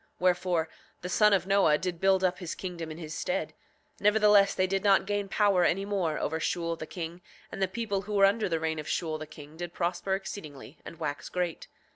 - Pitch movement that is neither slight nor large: Yes, average, 3.4 semitones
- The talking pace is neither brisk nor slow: No, fast, 220 wpm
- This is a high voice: No, medium, 180 Hz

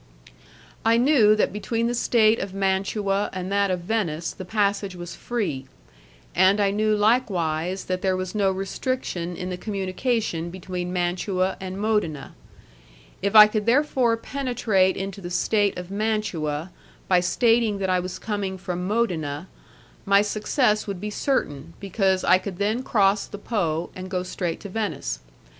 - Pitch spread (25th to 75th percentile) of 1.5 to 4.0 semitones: Yes, average, 2.9 semitones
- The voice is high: Yes, high, 195 Hz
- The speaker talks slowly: No, average, 155 wpm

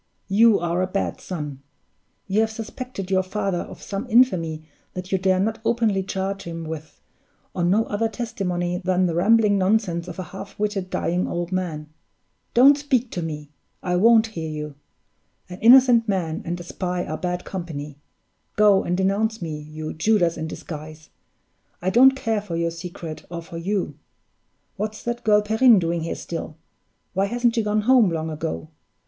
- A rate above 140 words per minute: Yes, average, 175 wpm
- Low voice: No, medium, 185 Hz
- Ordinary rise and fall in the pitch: Yes, average, 4.4 semitones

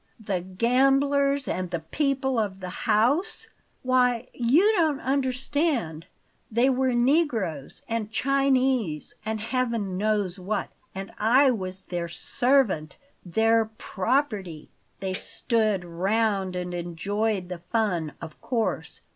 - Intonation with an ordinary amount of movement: No, wide, 5.9 semitones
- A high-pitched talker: Yes, high, 220 Hz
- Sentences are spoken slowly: Yes, slow, 115 wpm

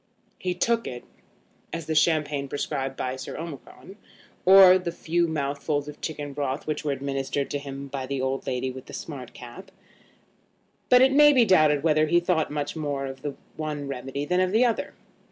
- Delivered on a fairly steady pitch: No, average, 3.9 semitones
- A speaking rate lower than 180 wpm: No, average, 190 wpm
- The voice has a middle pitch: Yes, medium, 150 Hz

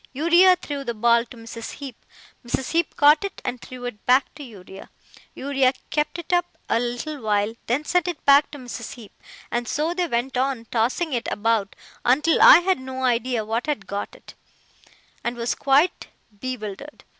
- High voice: Yes, very high, 255 Hz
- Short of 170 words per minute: No, average, 180 wpm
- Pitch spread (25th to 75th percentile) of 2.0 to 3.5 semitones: No, average, 4.3 semitones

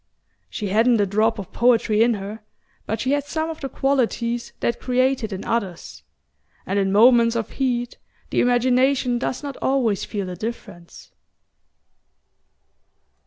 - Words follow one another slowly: No, average, 150 wpm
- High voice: Yes, high, 235 Hz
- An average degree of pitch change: Yes, average, 3.4 semitones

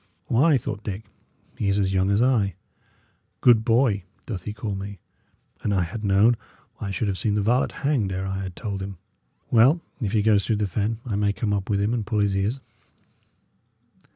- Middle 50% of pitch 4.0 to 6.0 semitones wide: No, narrow, 2.5 semitones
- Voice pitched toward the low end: Yes, low, 105 Hz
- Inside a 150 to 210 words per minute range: Yes, fast, 205 wpm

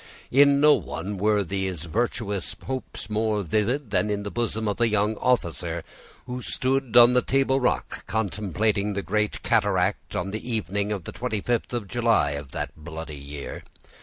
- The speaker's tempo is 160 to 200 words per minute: Yes, average, 165 wpm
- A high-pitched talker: No, low, 105 Hz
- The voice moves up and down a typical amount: Yes, average, 4.0 semitones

